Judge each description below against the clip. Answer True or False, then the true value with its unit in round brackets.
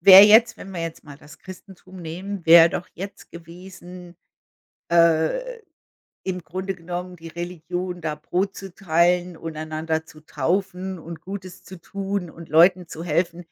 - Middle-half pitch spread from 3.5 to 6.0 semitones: False (2.4 semitones)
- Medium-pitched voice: True (175 Hz)